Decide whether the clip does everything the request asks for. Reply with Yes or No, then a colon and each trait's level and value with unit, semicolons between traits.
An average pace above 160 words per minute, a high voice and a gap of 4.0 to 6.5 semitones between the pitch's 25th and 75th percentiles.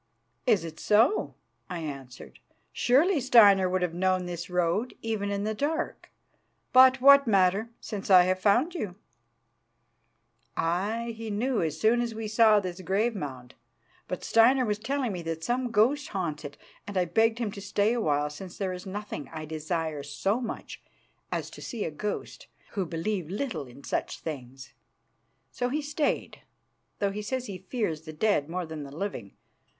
Yes: average, 170 wpm; high, 200 Hz; wide, 5.6 semitones